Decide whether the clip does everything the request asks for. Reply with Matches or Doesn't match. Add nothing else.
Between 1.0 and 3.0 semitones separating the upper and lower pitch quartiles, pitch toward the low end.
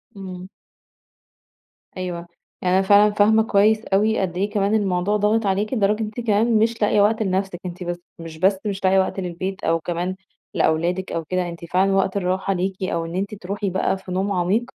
Doesn't match